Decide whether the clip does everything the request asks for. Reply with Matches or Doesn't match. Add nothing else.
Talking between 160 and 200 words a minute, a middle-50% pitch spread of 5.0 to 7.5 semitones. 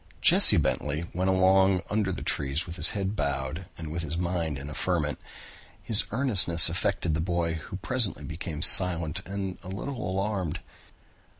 Doesn't match